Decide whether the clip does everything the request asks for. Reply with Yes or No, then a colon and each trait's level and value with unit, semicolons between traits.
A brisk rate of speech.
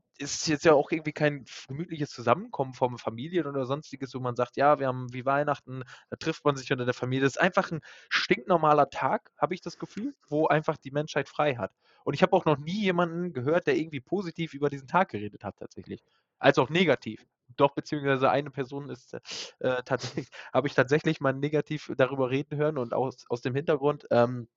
Yes: fast, 205 wpm